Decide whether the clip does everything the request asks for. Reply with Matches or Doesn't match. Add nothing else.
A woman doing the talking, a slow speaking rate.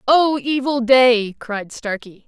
Matches